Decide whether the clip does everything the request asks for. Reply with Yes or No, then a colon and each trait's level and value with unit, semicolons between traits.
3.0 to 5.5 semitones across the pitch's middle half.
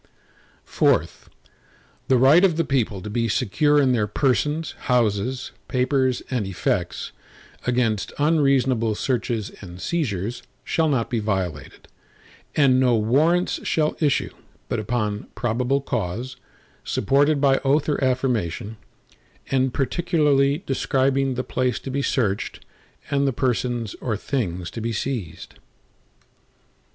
Yes: average, 4.0 semitones